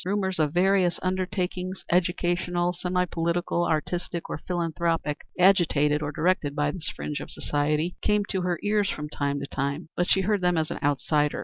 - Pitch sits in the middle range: Yes, medium, 175 Hz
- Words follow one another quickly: No, average, 175 wpm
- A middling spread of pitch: Yes, average, 3.3 semitones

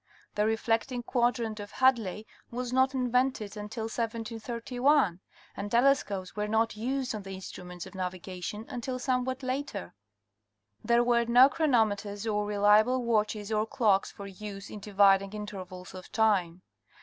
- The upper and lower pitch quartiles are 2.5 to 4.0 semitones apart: Yes, average, 3.4 semitones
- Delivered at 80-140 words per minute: Yes, slow, 135 wpm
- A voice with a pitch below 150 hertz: No, high, 220 Hz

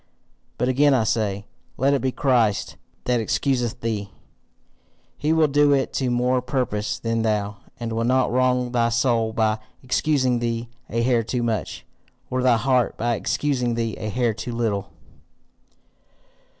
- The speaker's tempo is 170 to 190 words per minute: No, average, 155 wpm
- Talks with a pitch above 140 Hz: No, low, 120 Hz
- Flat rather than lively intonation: Yes, narrow, 2.3 semitones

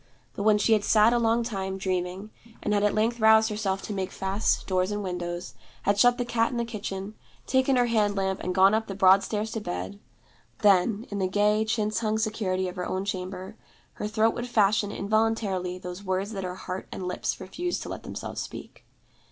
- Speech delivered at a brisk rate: Yes, fast, 210 wpm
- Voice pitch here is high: Yes, high, 205 Hz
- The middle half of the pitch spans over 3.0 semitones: No, average, 2.7 semitones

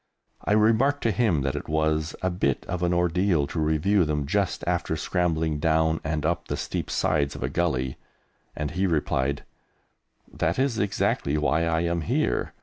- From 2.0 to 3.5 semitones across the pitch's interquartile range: Yes, average, 3.1 semitones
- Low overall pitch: Yes, very low, 80 Hz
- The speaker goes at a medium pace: Yes, average, 175 wpm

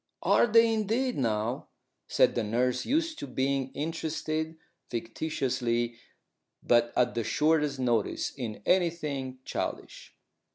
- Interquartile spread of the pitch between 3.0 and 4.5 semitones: No, average, 5.3 semitones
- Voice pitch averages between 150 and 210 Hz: No, low, 135 Hz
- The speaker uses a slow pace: Yes, slow, 115 wpm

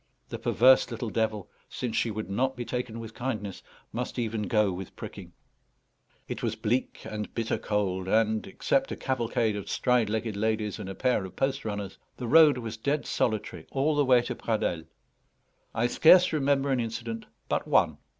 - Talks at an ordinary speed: Yes, average, 180 wpm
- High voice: No, low, 115 Hz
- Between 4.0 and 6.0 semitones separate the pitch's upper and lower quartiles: No, average, 3.2 semitones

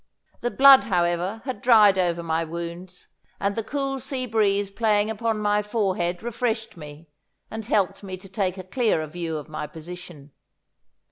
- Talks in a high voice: Yes, high, 200 Hz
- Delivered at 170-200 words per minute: No, average, 160 wpm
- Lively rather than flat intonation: No, average, 4.4 semitones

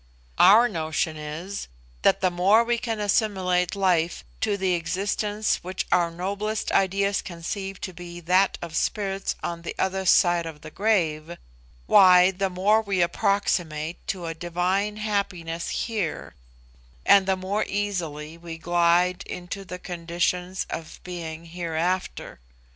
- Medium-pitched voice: Yes, medium, 180 Hz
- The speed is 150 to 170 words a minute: No, average, 140 wpm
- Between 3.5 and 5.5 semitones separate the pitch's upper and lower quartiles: No, average, 2.8 semitones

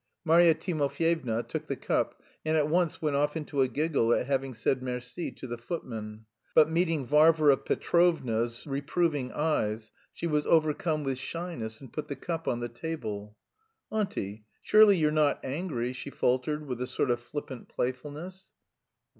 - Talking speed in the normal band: Yes, average, 165 wpm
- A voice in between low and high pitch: Yes, medium, 145 Hz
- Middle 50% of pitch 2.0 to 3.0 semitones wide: No, average, 4.6 semitones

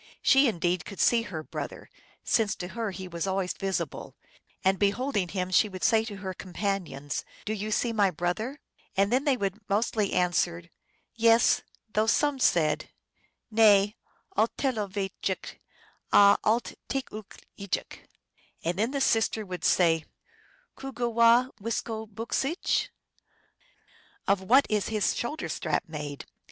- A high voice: Yes, high, 205 Hz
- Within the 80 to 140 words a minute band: No, average, 155 wpm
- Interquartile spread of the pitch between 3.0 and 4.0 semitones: Yes, average, 3.7 semitones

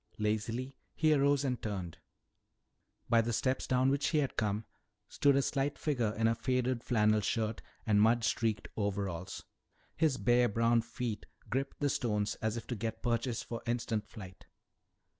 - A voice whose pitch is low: Yes, low, 115 Hz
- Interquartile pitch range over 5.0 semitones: No, average, 3.2 semitones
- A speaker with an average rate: Yes, average, 160 wpm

